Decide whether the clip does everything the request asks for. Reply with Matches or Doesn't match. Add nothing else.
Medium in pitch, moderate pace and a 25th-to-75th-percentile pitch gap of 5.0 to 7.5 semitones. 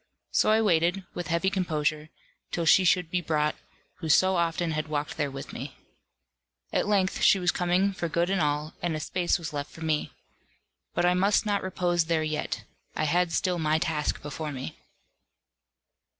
Doesn't match